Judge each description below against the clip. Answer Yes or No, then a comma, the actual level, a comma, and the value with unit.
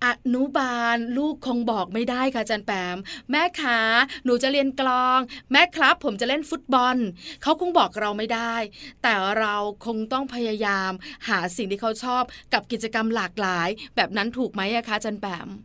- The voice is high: Yes, high, 235 Hz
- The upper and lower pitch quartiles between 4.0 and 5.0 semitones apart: No, average, 3.6 semitones